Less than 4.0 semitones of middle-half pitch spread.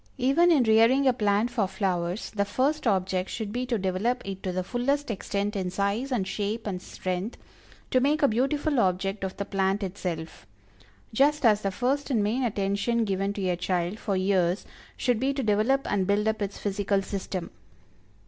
No: average, 4.3 semitones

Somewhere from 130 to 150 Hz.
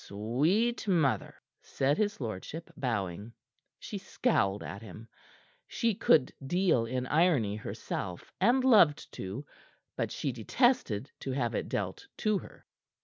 Yes: low, 135 Hz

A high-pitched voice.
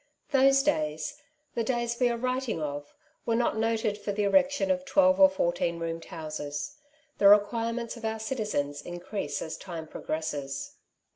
Yes: high, 220 Hz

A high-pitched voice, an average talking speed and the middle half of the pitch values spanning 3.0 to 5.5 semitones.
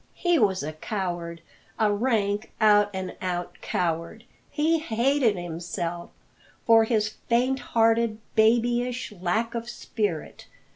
No: high, 215 Hz; slow, 115 wpm; average, 4.6 semitones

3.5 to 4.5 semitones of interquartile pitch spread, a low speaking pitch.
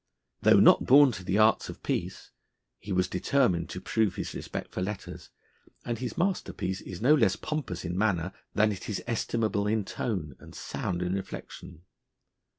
Yes: average, 4.0 semitones; low, 100 Hz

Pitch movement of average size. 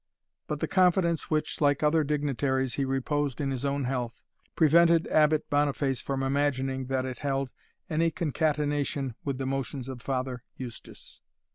No: narrow, 2.3 semitones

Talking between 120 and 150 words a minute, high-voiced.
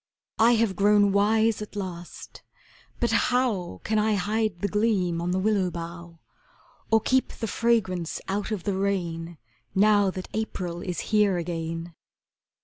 Yes: average, 145 wpm; high, 200 Hz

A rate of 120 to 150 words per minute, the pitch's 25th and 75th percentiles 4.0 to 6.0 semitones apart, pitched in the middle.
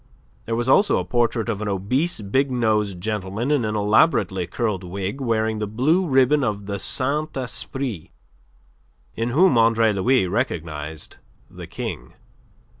No: average, 145 wpm; average, 4.7 semitones; low, 110 Hz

